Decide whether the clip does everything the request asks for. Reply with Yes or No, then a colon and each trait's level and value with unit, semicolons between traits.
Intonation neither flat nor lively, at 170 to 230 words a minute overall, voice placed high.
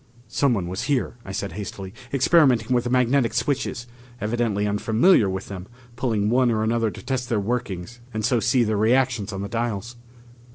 No: average, 3.4 semitones; average, 175 wpm; low, 115 Hz